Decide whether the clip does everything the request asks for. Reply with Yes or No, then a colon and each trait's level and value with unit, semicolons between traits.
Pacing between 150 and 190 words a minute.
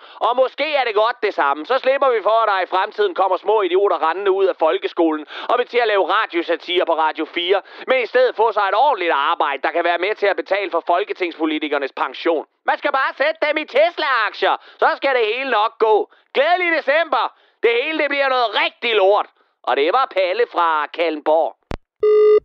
No: average, 205 wpm